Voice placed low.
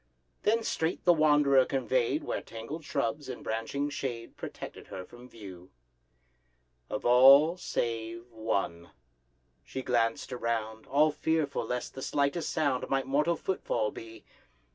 Yes: low, 130 Hz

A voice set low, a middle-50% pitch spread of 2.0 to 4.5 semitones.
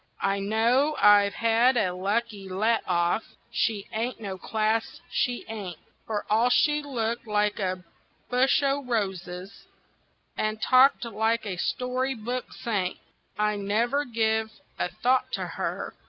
No: high, 220 Hz; average, 3.4 semitones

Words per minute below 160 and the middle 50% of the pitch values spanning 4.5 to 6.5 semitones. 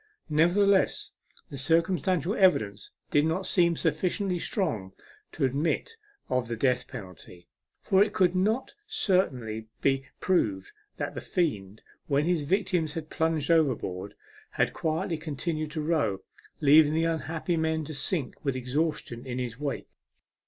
Yes: average, 140 wpm; average, 5.2 semitones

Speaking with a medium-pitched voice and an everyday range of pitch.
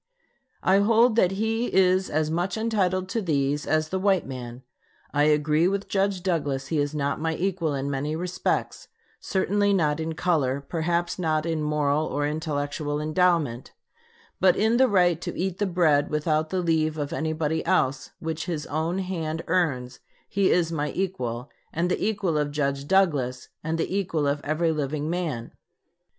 Yes: medium, 160 Hz; average, 4.0 semitones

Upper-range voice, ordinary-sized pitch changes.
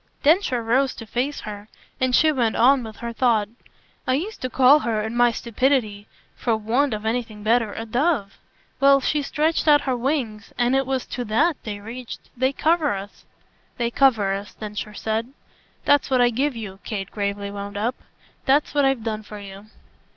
Yes: high, 240 Hz; average, 4.0 semitones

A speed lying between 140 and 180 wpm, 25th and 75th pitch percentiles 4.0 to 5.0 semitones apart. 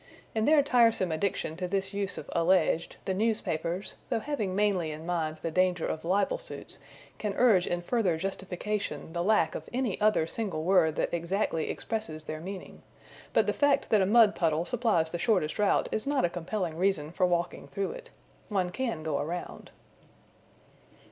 Yes: average, 175 wpm; average, 4.3 semitones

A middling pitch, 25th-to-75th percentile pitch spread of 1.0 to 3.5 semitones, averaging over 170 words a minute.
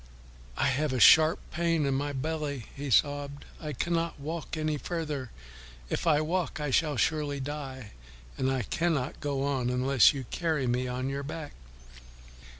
No: medium, 145 Hz; average, 2.8 semitones; average, 160 wpm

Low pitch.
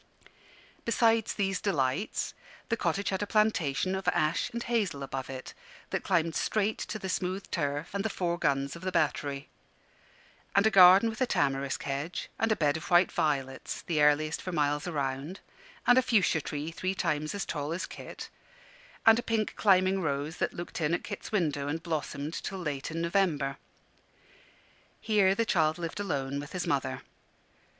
No: medium, 170 Hz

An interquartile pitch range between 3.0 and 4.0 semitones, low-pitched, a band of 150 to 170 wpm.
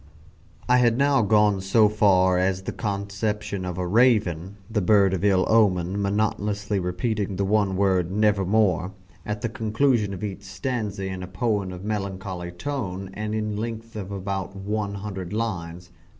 No: narrow, 2.4 semitones; low, 100 Hz; average, 155 wpm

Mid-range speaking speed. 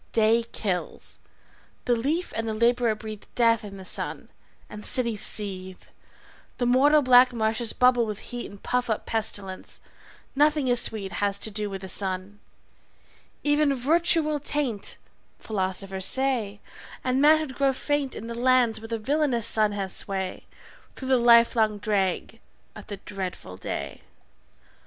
Yes: average, 150 wpm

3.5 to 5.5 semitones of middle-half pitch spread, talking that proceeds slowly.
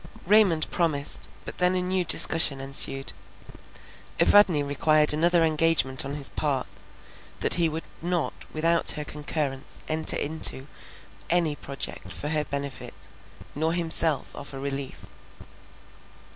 No: average, 2.9 semitones; slow, 120 wpm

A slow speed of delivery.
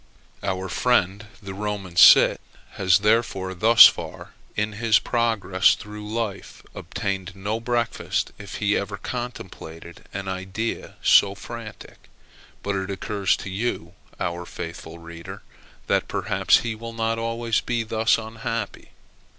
Yes: slow, 130 wpm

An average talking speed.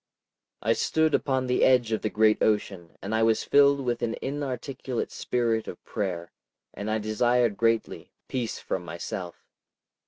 Yes: average, 150 wpm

